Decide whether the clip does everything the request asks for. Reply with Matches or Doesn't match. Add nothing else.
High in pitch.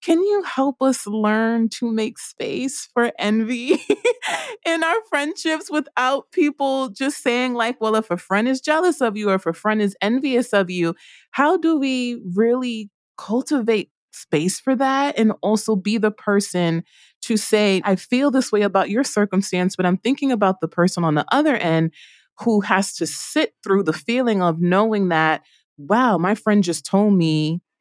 Matches